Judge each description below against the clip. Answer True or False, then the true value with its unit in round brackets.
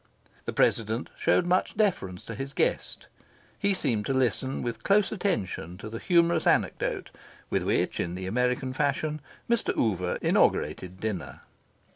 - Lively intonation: True (8.5 semitones)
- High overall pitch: False (125 Hz)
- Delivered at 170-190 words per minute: False (145 wpm)